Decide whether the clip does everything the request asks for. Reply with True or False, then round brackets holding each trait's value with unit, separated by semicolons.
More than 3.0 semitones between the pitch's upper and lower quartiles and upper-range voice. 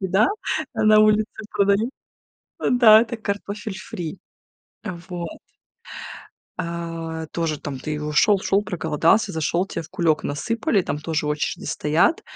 False (4.9 semitones; 180 Hz)